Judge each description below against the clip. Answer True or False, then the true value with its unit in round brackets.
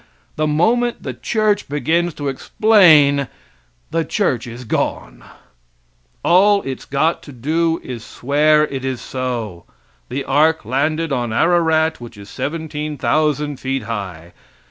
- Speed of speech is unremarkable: False (125 wpm)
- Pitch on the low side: False (145 Hz)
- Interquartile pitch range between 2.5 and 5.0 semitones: True (4.2 semitones)